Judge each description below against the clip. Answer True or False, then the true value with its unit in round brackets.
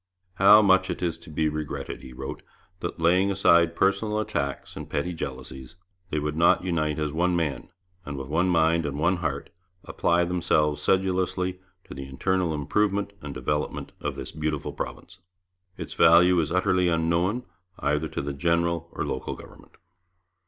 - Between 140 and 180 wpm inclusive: True (165 wpm)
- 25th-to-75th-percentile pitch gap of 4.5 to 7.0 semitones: False (3.5 semitones)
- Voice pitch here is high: False (85 Hz)